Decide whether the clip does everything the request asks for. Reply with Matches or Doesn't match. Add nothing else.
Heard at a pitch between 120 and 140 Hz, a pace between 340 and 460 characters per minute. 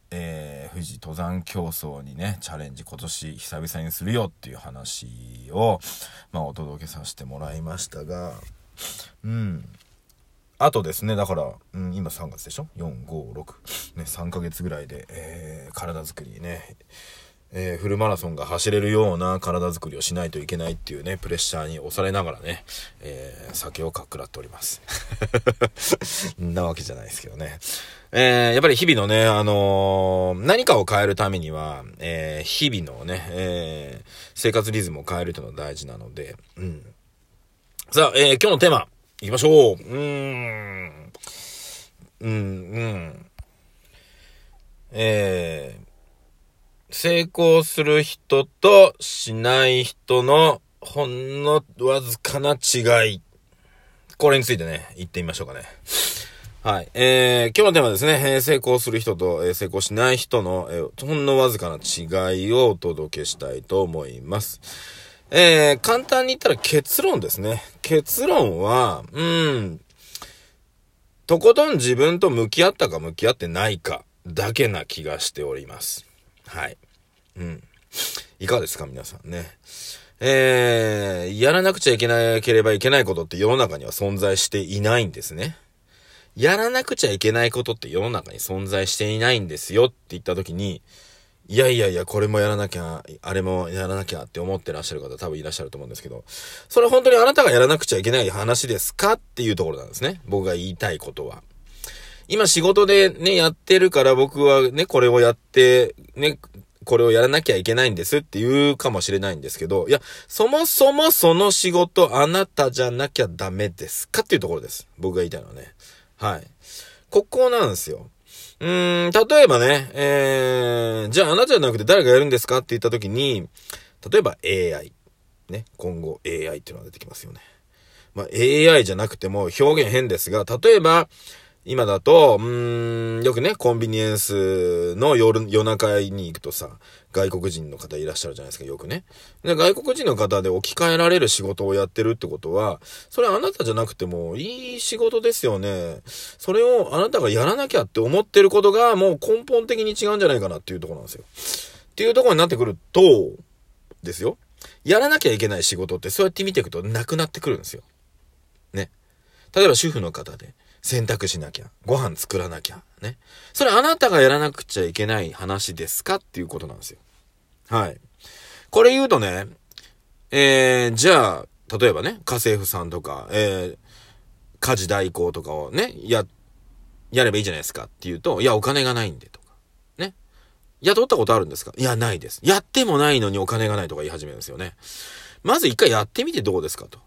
Doesn't match